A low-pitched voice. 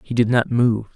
Yes: low, 115 Hz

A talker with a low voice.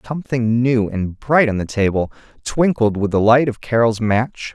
Yes: low, 115 Hz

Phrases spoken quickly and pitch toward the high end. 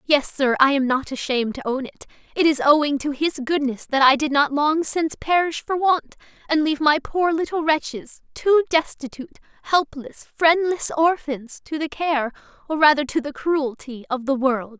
No: average, 185 wpm; very high, 290 Hz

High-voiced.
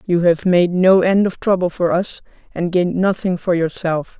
No: medium, 180 Hz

